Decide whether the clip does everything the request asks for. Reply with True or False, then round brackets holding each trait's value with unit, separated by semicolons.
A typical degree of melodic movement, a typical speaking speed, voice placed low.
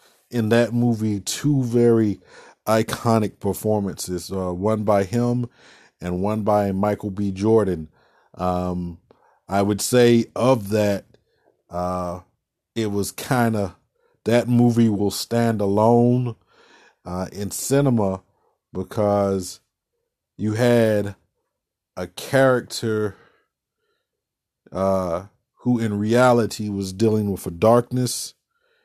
False (3.7 semitones; 105 wpm; 105 Hz)